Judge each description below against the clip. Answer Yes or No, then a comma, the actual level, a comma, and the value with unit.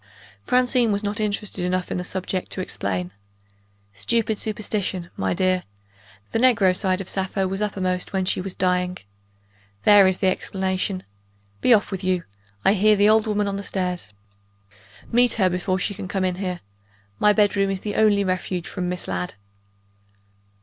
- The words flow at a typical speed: Yes, average, 170 wpm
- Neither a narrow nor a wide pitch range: No, narrow, 2.2 semitones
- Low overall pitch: No, high, 190 Hz